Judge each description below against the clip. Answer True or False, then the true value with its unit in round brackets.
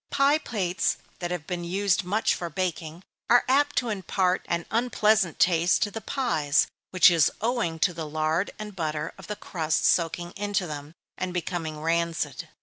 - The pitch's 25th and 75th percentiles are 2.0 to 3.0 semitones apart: False (4.0 semitones)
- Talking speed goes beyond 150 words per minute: True (170 wpm)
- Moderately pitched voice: True (180 Hz)